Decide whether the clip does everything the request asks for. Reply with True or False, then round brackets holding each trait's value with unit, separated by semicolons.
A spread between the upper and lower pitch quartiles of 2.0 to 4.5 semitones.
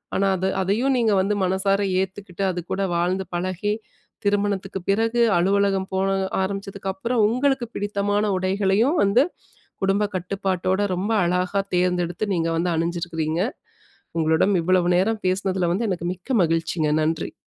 True (2.4 semitones)